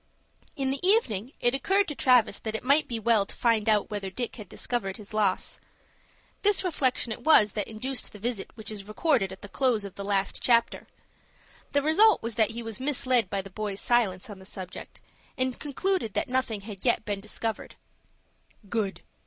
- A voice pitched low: No, high, 225 Hz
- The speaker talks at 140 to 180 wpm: No, average, 195 wpm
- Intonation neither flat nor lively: Yes, average, 4.2 semitones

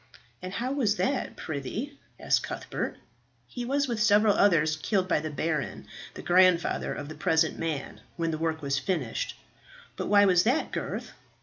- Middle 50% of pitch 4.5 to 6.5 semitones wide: Yes, wide, 5.5 semitones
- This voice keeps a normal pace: Yes, average, 170 wpm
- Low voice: No, medium, 180 Hz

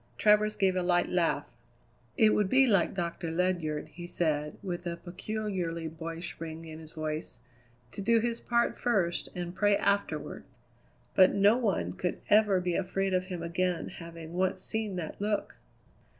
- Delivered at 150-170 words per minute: Yes, average, 165 wpm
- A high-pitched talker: No, medium, 180 Hz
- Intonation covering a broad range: No, average, 3.5 semitones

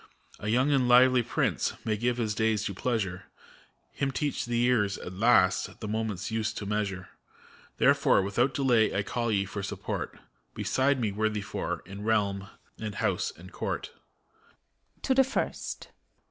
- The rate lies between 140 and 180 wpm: Yes, average, 160 wpm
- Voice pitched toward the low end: Yes, low, 110 Hz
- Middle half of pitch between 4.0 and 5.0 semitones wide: No, average, 3.5 semitones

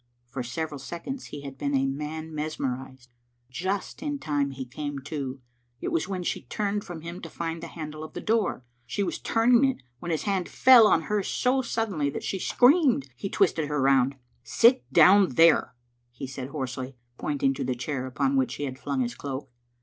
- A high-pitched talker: No, medium, 150 Hz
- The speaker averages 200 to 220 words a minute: Yes, fast, 205 wpm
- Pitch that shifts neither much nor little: No, wide, 6.3 semitones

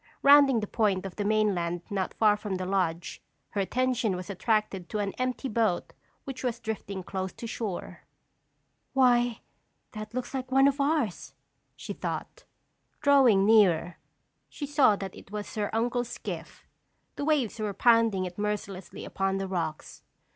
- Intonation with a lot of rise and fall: No, average, 4.3 semitones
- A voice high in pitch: Yes, high, 215 Hz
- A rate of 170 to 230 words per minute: No, average, 155 wpm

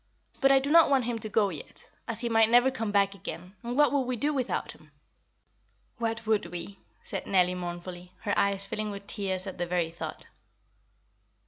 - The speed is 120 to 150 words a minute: No, average, 200 wpm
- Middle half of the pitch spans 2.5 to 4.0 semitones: No, average, 4.5 semitones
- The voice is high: Yes, high, 210 Hz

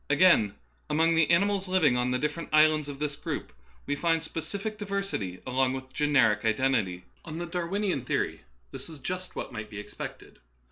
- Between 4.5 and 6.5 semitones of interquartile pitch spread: Yes, average, 5.3 semitones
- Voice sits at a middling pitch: Yes, medium, 150 Hz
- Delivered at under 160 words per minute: No, average, 185 wpm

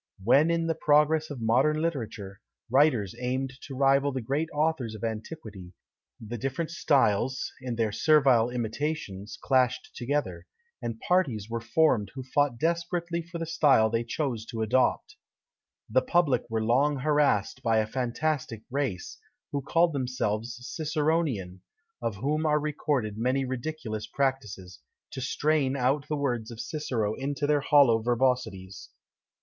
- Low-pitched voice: Yes, low, 130 Hz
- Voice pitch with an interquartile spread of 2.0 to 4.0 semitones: No, average, 4.9 semitones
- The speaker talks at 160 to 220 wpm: No, average, 145 wpm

